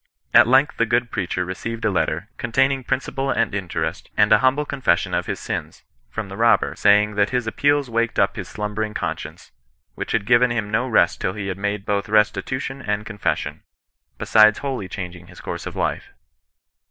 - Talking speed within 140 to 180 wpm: No, average, 190 wpm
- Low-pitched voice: Yes, low, 110 Hz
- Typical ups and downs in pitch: Yes, average, 3.4 semitones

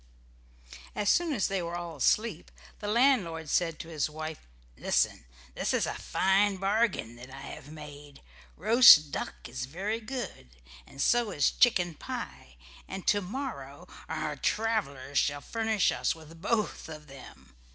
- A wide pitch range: Yes, wide, 6.7 semitones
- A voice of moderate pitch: Yes, medium, 170 Hz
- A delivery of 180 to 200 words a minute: No, average, 150 wpm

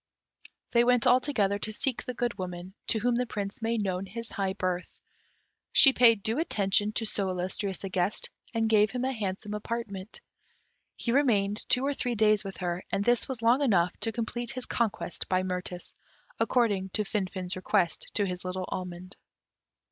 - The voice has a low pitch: No, high, 210 Hz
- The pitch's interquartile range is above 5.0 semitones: No, average, 4.0 semitones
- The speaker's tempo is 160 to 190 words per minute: Yes, average, 180 wpm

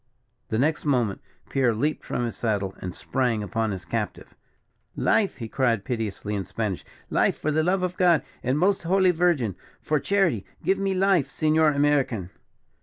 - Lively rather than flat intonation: Yes, wide, 7.4 semitones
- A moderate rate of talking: Yes, average, 180 wpm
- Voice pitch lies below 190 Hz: Yes, low, 135 Hz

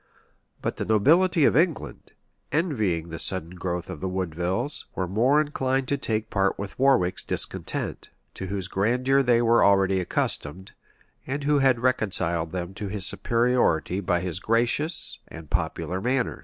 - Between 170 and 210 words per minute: No, average, 155 wpm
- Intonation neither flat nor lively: No, wide, 6.1 semitones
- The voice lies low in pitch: Yes, low, 105 Hz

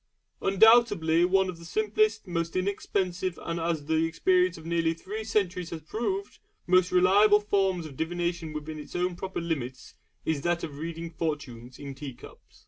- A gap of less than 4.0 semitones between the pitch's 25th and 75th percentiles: Yes, average, 3.2 semitones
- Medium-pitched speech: Yes, medium, 170 Hz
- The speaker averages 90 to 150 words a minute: No, average, 165 wpm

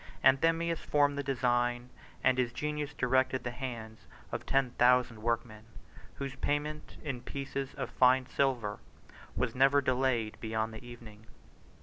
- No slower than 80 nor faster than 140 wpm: Yes, slow, 135 wpm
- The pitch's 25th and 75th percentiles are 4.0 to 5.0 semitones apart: No, narrow, 2.6 semitones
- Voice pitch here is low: Yes, low, 130 Hz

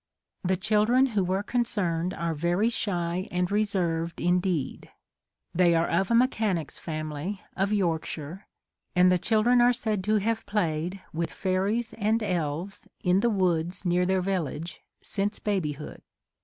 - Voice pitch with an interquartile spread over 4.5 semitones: No, average, 3.7 semitones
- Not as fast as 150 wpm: No, average, 155 wpm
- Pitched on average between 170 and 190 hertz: Yes, medium, 185 Hz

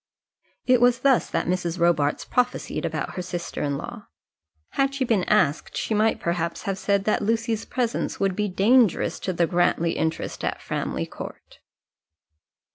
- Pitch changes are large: No, average, 5.0 semitones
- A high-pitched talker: Yes, high, 195 Hz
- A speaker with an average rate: Yes, average, 160 wpm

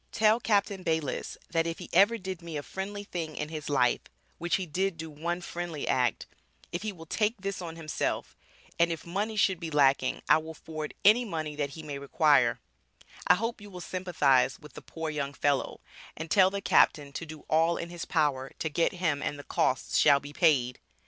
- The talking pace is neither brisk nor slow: No, fast, 210 wpm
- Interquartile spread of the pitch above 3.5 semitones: Yes, average, 4.0 semitones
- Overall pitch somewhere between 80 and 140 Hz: No, medium, 165 Hz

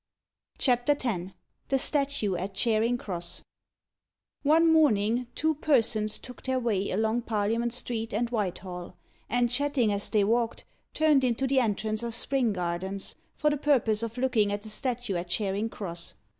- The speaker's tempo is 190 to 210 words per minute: No, average, 155 wpm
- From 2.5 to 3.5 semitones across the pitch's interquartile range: No, average, 4.1 semitones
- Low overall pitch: No, high, 230 Hz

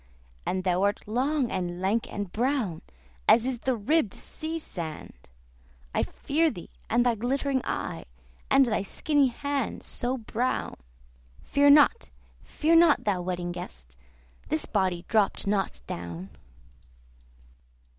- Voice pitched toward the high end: Yes, high, 225 Hz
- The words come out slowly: Yes, slow, 130 wpm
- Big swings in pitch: Yes, wide, 7.3 semitones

